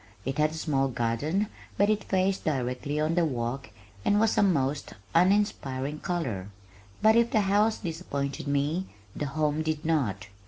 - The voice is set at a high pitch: No, medium, 155 Hz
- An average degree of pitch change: No, wide, 5.8 semitones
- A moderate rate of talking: Yes, average, 160 wpm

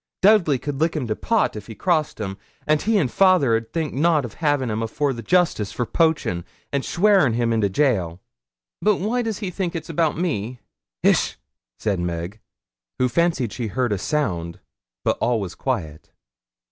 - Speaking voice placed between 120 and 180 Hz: Yes, low, 135 Hz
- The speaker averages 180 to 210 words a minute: Yes, average, 185 wpm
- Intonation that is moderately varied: No, wide, 7.6 semitones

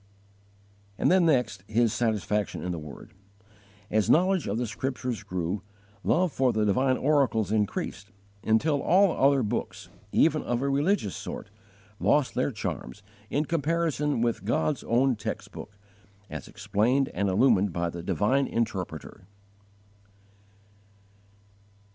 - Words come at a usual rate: No, slow, 125 wpm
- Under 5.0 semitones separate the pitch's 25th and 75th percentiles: No, wide, 5.4 semitones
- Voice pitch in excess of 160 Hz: No, low, 115 Hz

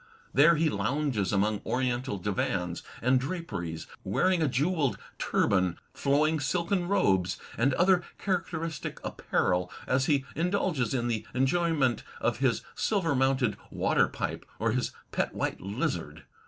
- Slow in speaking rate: Yes, slow, 130 wpm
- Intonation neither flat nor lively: No, wide, 7.4 semitones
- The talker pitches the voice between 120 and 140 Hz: Yes, low, 135 Hz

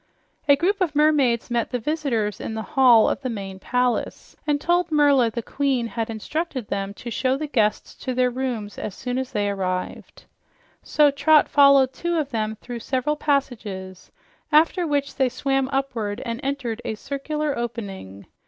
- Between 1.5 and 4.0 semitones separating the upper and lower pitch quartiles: No, average, 4.4 semitones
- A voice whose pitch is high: Yes, very high, 255 Hz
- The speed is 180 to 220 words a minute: No, average, 170 wpm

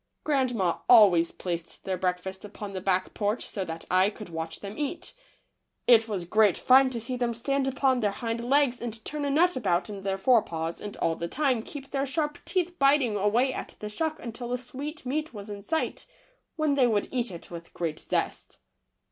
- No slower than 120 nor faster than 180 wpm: No, average, 200 wpm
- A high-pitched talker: Yes, high, 230 Hz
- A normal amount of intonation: No, wide, 5.8 semitones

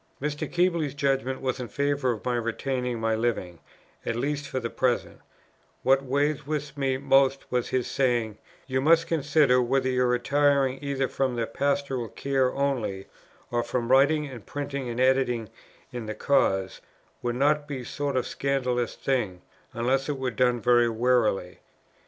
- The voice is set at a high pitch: No, low, 130 Hz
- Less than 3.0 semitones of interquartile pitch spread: Yes, narrow, 2.6 semitones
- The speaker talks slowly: No, average, 165 wpm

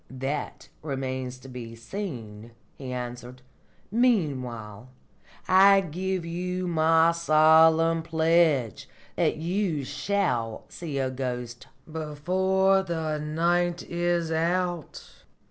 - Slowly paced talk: Yes, slow, 95 wpm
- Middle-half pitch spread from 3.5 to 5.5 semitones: Yes, average, 5.2 semitones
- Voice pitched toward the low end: No, medium, 160 Hz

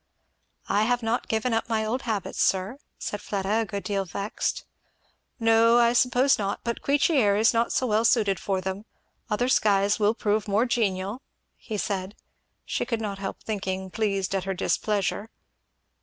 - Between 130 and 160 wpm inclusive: No, average, 170 wpm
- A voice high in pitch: Yes, high, 215 Hz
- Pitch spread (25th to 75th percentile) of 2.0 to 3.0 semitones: Yes, average, 2.7 semitones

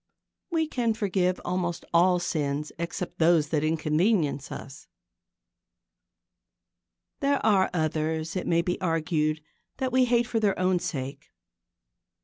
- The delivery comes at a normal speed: No, slow, 125 wpm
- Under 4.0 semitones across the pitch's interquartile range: No, average, 4.3 semitones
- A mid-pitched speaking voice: Yes, medium, 175 Hz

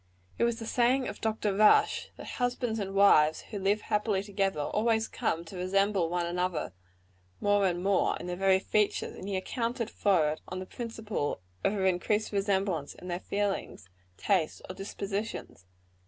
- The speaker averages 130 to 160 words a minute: No, average, 170 wpm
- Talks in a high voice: Yes, high, 195 Hz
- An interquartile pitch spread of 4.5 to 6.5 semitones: No, average, 2.9 semitones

